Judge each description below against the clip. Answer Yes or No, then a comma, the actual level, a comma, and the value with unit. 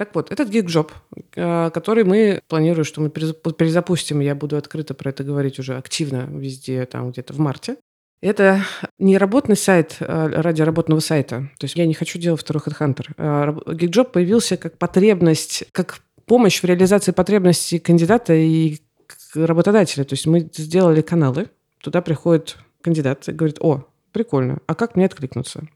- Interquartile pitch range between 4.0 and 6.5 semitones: No, average, 3.4 semitones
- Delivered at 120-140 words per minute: No, average, 155 wpm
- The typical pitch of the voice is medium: Yes, medium, 160 Hz